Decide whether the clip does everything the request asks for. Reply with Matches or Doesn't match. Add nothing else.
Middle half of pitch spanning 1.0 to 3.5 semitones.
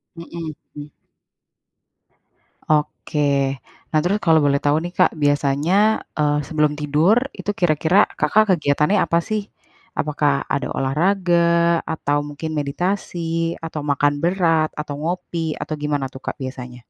Matches